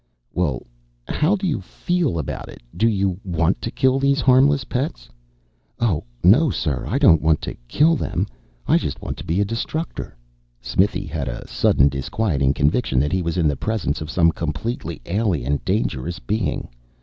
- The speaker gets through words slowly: No, average, 175 wpm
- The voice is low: Yes, very low, 90 Hz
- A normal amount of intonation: No, wide, 8.3 semitones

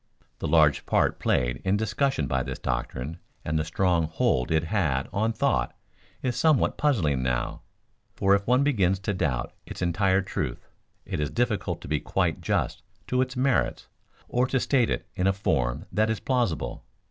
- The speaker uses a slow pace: No, average, 175 wpm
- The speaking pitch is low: Yes, very low, 95 Hz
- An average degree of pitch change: No, wide, 7.8 semitones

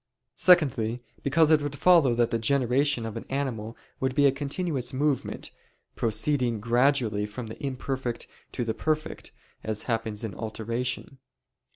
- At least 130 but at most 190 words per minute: Yes, average, 145 wpm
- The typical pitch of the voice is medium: No, low, 125 Hz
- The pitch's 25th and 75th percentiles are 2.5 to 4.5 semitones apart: Yes, average, 3.8 semitones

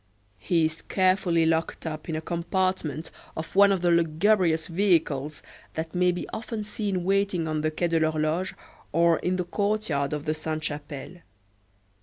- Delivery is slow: No, average, 165 wpm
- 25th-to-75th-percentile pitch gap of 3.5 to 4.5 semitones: No, average, 3.0 semitones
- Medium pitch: Yes, medium, 165 Hz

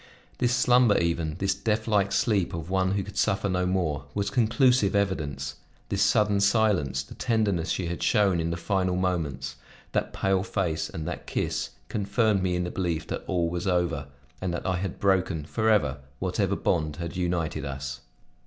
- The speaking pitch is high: No, very low, 90 Hz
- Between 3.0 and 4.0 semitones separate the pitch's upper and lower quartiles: Yes, average, 3.4 semitones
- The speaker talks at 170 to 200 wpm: Yes, average, 175 wpm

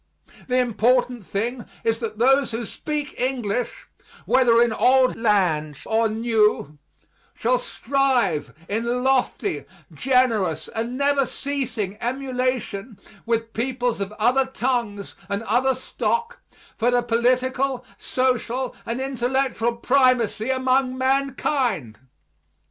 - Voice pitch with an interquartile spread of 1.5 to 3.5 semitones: Yes, average, 2.7 semitones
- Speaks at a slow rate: Yes, slow, 110 wpm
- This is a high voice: Yes, high, 245 Hz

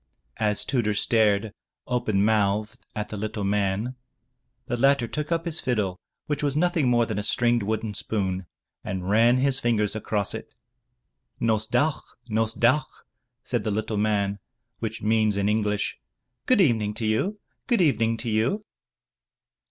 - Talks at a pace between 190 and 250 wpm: No, average, 150 wpm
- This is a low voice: Yes, low, 110 Hz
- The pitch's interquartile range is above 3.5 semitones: No, average, 3.0 semitones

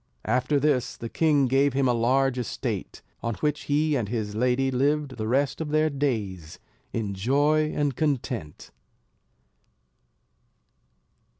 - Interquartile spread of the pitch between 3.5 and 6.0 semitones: Yes, average, 3.9 semitones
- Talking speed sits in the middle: No, slow, 130 wpm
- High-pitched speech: No, low, 135 Hz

